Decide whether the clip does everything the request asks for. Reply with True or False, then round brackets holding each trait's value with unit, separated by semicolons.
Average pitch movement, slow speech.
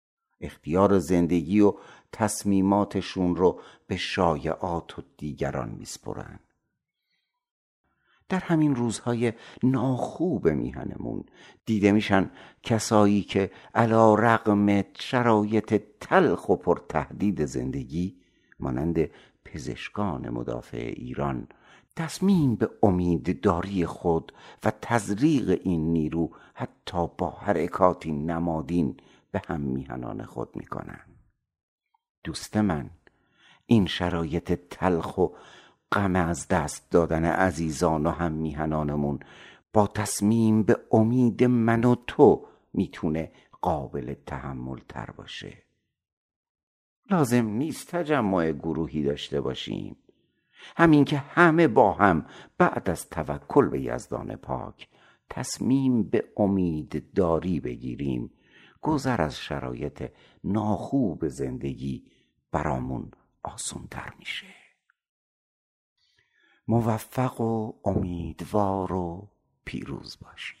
False (5.7 semitones; 95 wpm)